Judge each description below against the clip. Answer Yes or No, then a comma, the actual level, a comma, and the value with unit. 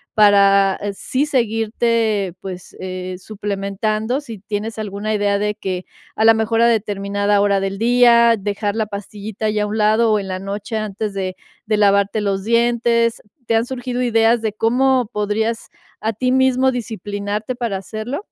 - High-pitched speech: Yes, high, 215 Hz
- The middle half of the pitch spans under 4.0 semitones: Yes, narrow, 2.5 semitones